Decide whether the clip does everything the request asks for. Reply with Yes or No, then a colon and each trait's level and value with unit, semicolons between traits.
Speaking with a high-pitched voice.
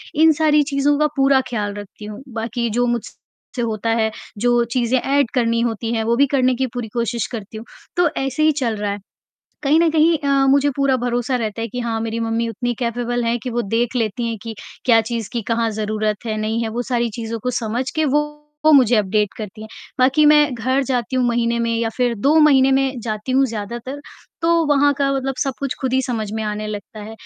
Yes: high, 240 Hz